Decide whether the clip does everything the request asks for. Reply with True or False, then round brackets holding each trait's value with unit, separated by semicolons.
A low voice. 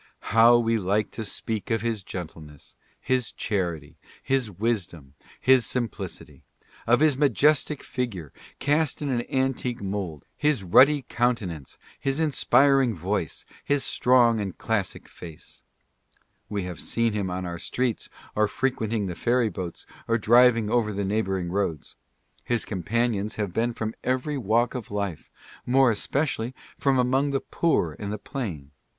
True (115 Hz)